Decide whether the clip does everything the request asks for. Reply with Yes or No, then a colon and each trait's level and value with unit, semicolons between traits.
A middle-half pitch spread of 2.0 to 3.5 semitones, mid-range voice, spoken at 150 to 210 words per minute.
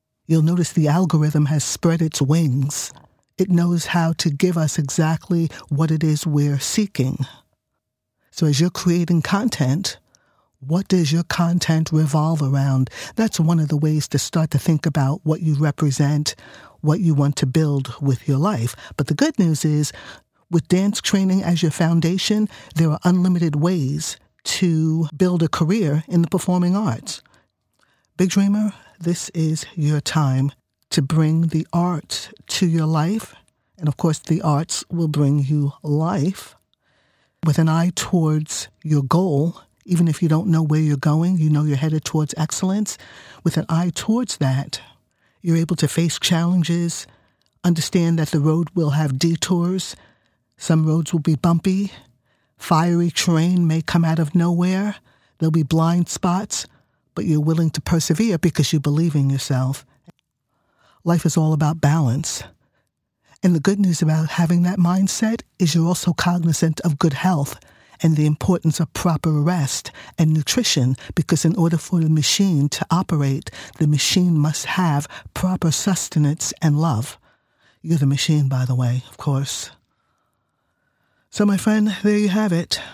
Yes: average, 2.8 semitones; medium, 160 Hz; average, 160 wpm